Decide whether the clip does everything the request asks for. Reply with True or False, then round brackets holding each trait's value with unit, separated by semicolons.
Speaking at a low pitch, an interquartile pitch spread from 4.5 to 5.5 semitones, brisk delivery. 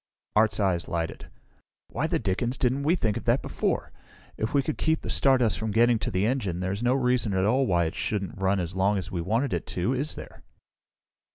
True (110 Hz; 5.1 semitones; 215 wpm)